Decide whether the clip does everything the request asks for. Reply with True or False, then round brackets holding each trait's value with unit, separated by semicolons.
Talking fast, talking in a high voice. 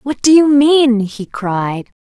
False (175 wpm; 245 Hz)